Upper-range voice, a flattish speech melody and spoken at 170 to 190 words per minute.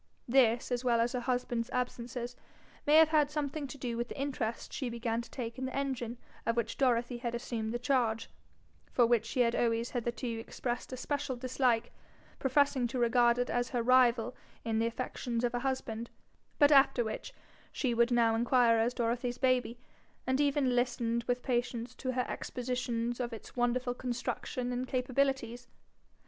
Yes: high, 245 Hz; narrow, 1.6 semitones; average, 175 wpm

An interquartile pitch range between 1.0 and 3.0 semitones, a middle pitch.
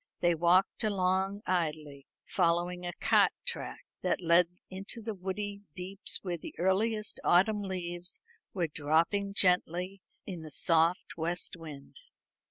Yes: narrow, 2.6 semitones; medium, 180 Hz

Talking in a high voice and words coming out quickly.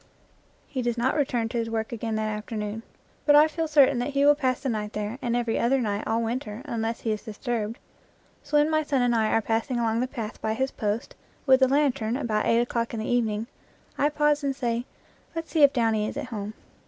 Yes: high, 235 Hz; fast, 235 wpm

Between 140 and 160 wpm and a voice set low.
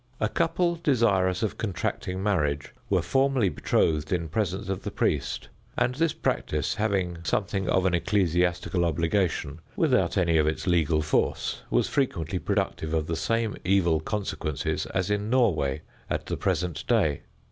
Yes: average, 150 wpm; very low, 90 Hz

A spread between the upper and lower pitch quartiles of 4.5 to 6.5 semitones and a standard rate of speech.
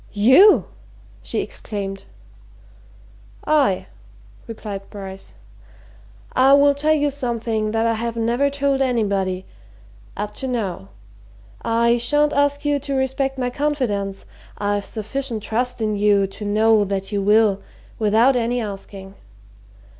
No: average, 4.8 semitones; slow, 125 wpm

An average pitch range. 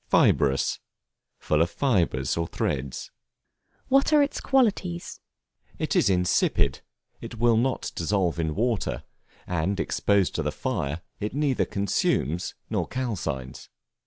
No: wide, 8.2 semitones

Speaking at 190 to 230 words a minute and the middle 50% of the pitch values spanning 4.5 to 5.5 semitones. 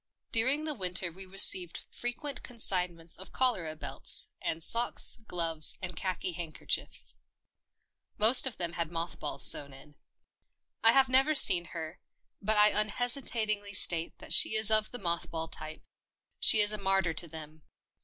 No: average, 165 wpm; average, 5.2 semitones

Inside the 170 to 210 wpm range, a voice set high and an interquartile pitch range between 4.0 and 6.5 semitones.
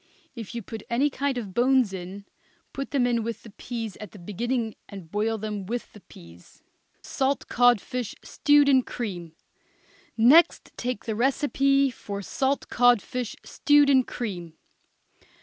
No: average, 150 wpm; high, 235 Hz; average, 4.4 semitones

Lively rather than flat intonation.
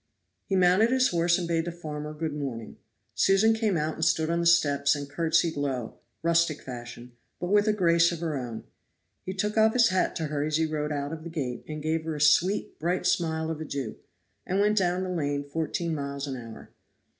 No: average, 3.6 semitones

